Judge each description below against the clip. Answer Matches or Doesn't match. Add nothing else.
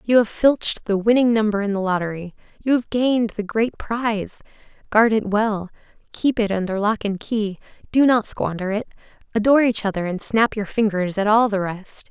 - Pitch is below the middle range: Doesn't match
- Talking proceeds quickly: Doesn't match